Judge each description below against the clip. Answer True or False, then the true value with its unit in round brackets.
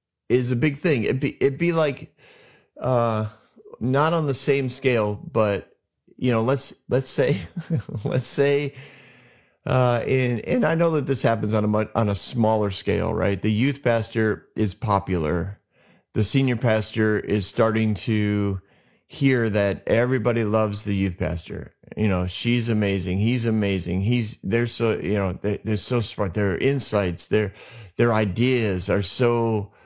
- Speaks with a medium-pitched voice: False (115 Hz)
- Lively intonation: False (3.7 semitones)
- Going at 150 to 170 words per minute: True (160 wpm)